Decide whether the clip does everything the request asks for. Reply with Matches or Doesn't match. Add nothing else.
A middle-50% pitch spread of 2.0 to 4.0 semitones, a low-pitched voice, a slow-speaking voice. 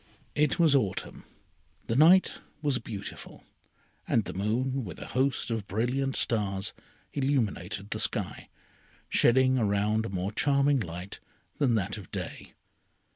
Doesn't match